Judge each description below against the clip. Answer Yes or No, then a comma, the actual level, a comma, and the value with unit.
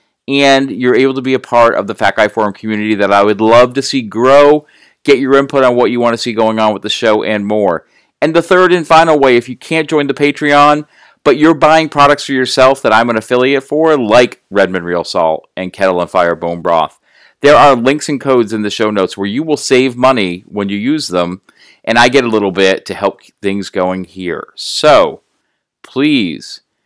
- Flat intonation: No, wide, 5.6 semitones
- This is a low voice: Yes, low, 125 Hz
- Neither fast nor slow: No, fast, 225 wpm